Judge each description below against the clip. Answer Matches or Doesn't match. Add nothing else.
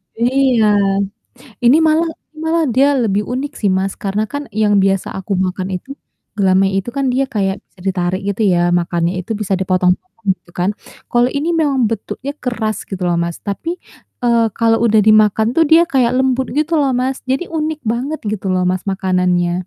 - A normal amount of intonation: Doesn't match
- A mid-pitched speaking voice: Doesn't match